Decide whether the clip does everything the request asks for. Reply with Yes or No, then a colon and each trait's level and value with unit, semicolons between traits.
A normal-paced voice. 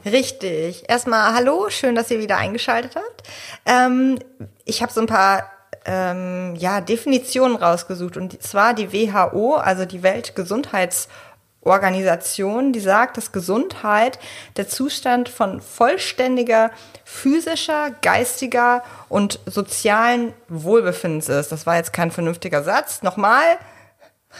No: slow, 115 wpm